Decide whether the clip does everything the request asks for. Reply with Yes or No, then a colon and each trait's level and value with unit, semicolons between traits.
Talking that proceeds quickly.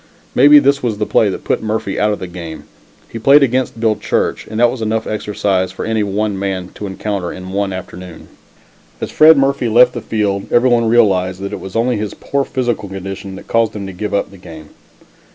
Yes: fast, 215 wpm